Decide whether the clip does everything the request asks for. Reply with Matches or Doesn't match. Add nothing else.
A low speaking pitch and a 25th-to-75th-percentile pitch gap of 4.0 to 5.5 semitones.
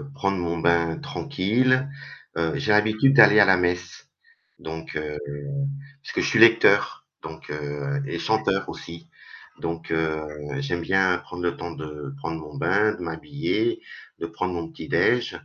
Matches